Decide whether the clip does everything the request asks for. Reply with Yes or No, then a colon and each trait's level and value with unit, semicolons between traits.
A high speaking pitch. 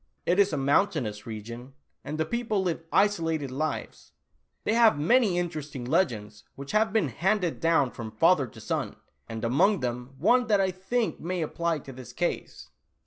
No: medium, 160 Hz